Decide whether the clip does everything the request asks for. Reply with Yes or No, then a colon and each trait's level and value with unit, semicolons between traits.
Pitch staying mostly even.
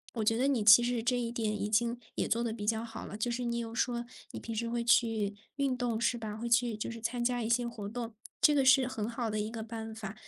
Yes: narrow, 1.5 semitones